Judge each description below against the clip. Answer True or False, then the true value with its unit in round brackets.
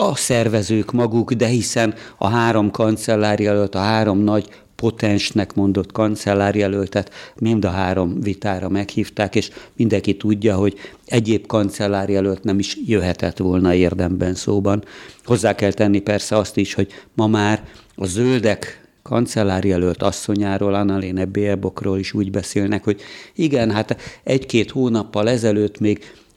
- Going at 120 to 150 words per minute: True (125 wpm)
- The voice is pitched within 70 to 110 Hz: True (105 Hz)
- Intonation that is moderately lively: False (2.1 semitones)